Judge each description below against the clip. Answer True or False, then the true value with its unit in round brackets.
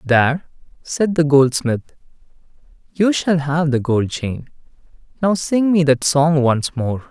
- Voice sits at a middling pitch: True (150 Hz)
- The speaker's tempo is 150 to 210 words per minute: False (135 wpm)